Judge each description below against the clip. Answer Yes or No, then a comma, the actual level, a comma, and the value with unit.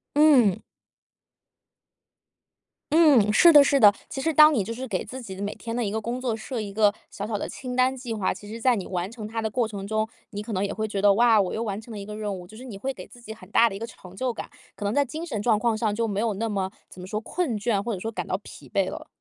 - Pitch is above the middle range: Yes, high, 220 Hz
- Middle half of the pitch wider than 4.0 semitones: No, average, 3.1 semitones